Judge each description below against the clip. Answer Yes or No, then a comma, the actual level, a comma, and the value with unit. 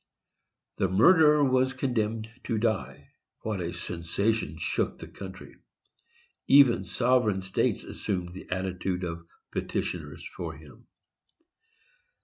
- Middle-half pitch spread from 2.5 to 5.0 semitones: No, wide, 5.6 semitones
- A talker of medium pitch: No, low, 105 Hz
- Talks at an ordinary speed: No, slow, 105 wpm